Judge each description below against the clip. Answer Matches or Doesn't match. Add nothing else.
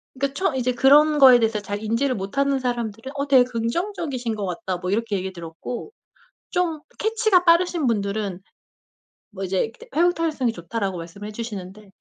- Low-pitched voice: Doesn't match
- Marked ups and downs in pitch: Matches